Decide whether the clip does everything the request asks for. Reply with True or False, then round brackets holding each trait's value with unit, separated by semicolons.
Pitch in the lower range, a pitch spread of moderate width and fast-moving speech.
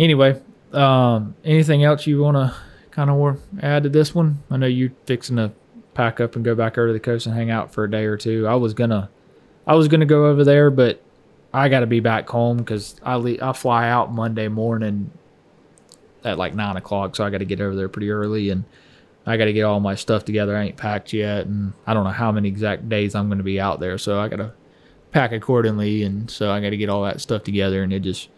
True (110 Hz; 3.9 semitones; 235 wpm)